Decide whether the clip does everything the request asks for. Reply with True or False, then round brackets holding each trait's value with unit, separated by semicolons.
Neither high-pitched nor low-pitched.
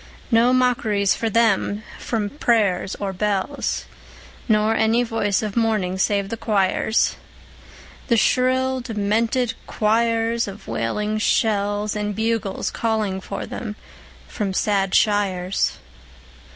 False (215 Hz)